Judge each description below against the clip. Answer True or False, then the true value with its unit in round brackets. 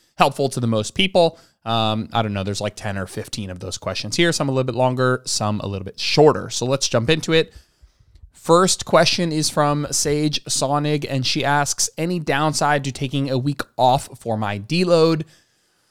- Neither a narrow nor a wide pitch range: False (6.0 semitones)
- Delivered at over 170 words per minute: True (195 wpm)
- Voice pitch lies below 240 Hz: True (135 Hz)